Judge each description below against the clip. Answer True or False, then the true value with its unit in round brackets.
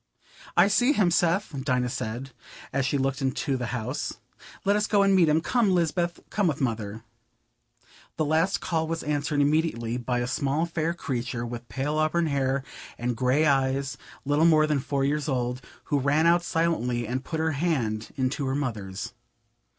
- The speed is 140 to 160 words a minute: False (175 wpm)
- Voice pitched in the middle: True (145 Hz)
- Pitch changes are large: False (4.4 semitones)